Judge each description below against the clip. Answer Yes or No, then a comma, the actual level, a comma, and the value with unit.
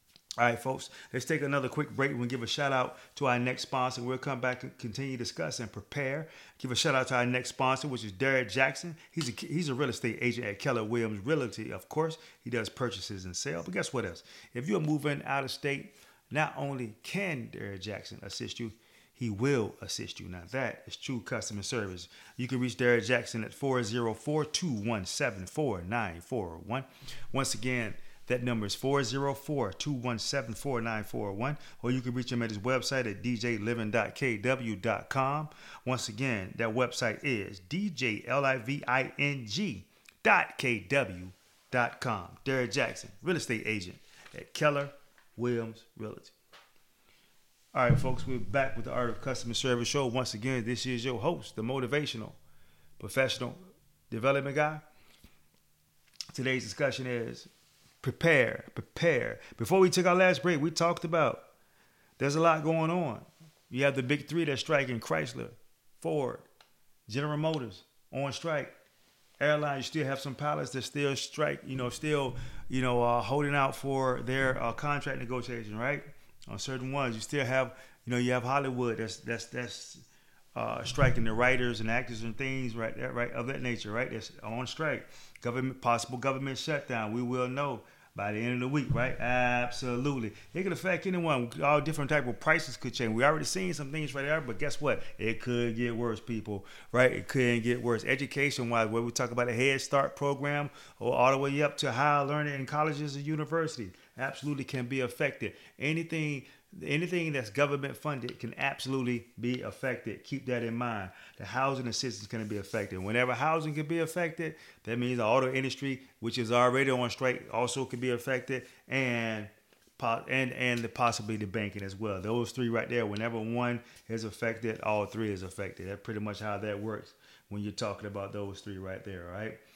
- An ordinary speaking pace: Yes, average, 175 wpm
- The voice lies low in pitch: Yes, low, 125 Hz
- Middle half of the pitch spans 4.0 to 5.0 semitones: No, average, 3.3 semitones